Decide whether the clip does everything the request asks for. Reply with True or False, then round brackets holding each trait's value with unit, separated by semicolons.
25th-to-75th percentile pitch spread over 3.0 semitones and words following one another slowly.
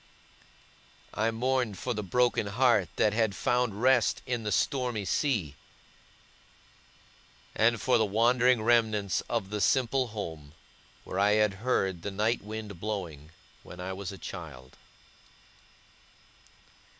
True (3.7 semitones; 125 wpm)